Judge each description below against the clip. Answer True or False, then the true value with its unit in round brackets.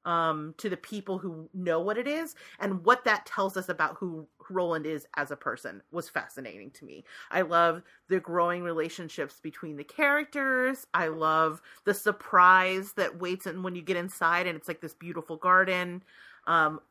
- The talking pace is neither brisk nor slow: True (180 wpm)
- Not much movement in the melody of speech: False (3.1 semitones)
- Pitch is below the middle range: False (180 Hz)